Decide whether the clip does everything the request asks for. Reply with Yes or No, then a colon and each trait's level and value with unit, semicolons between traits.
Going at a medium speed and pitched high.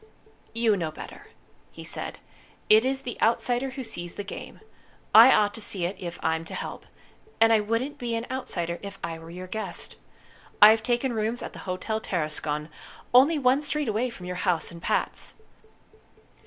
Yes: average, 180 wpm; high, 220 Hz